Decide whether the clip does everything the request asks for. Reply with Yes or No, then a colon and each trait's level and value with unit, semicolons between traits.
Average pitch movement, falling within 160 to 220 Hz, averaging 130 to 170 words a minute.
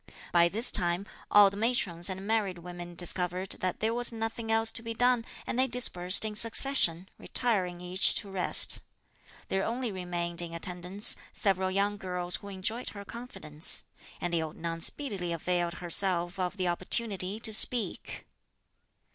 Yes: average, 4.1 semitones; high, 190 Hz; average, 160 wpm